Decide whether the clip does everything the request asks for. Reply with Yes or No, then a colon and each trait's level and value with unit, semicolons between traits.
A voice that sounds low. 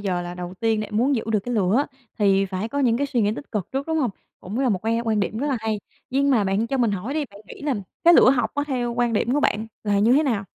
No: high, 225 Hz